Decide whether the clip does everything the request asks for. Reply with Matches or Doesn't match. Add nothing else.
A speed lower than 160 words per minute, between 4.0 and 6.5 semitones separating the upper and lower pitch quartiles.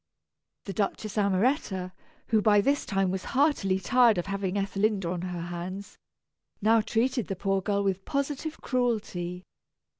Doesn't match